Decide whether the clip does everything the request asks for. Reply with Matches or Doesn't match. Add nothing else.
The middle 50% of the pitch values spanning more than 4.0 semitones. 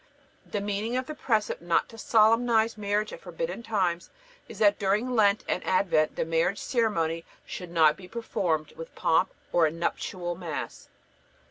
Matches